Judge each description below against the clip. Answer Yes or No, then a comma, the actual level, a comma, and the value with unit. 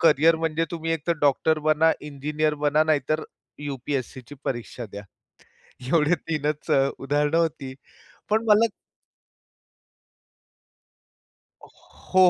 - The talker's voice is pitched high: No, medium, 150 Hz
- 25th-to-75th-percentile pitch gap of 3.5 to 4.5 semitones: No, narrow, 2.6 semitones